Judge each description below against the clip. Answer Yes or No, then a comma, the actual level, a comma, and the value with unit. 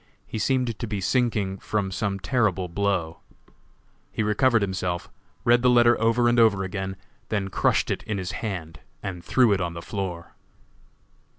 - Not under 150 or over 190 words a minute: Yes, average, 165 wpm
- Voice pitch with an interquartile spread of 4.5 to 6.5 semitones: No, average, 3.7 semitones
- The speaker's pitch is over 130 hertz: No, low, 100 Hz